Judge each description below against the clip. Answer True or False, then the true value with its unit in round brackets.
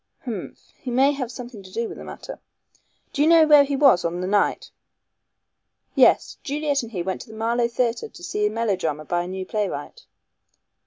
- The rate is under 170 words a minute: False (200 wpm)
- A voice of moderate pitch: False (235 Hz)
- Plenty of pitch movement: True (6.9 semitones)